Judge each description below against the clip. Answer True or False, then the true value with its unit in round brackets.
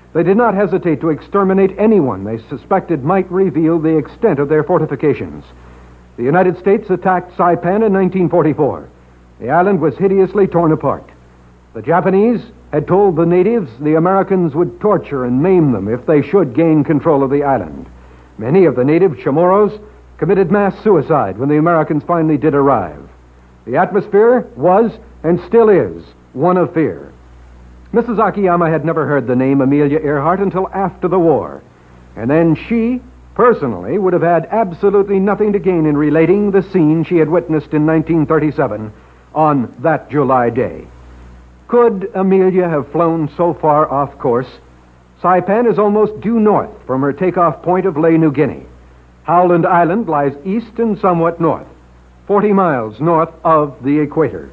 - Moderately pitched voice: True (160 Hz)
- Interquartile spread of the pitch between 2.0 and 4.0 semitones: False (5.5 semitones)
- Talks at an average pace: True (160 wpm)